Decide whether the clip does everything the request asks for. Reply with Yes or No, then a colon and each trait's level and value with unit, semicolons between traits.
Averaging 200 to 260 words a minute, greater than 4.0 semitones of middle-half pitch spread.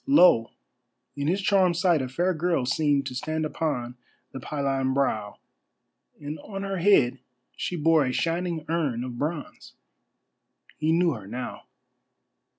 No: average, 145 wpm; average, 4.8 semitones